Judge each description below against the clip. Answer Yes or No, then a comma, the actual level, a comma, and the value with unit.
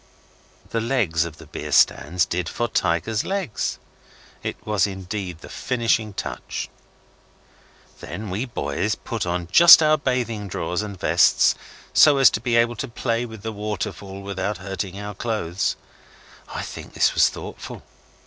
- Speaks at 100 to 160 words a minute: Yes, average, 150 wpm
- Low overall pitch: Yes, low, 105 Hz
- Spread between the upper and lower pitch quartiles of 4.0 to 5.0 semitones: Yes, average, 4.3 semitones